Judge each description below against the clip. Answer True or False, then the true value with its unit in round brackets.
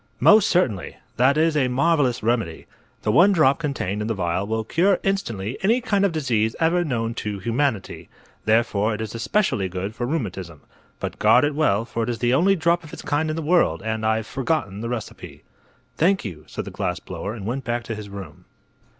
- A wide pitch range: True (7.0 semitones)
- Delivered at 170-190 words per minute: False (205 wpm)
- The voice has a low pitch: True (120 Hz)